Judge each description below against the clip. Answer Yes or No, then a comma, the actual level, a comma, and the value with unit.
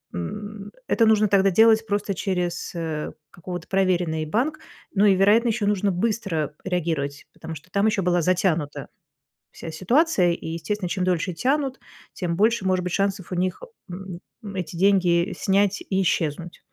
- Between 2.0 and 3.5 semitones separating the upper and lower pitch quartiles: Yes, average, 3.2 semitones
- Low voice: No, medium, 185 Hz